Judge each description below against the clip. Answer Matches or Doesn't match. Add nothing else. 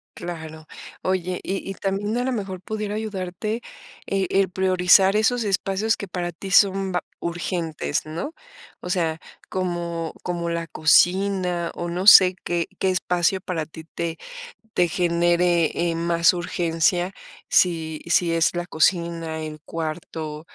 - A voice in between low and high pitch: Matches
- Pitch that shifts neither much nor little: Doesn't match